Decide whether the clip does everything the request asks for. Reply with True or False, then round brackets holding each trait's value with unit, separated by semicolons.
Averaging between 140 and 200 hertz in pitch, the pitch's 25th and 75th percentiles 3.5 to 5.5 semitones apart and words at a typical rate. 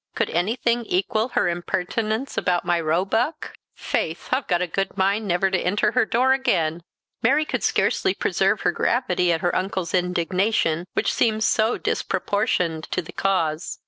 True (190 Hz; 4.1 semitones; 155 wpm)